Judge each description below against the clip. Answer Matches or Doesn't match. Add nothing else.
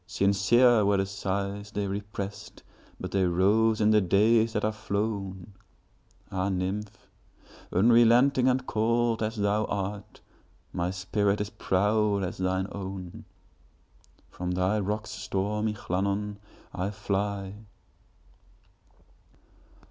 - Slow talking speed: Matches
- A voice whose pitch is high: Doesn't match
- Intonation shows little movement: Matches